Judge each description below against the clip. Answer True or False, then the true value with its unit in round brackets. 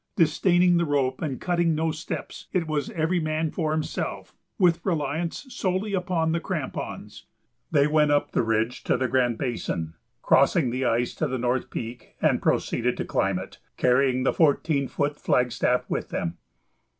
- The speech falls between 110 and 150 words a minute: False (165 wpm)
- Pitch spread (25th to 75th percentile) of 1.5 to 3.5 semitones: False (4.8 semitones)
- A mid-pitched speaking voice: True (150 Hz)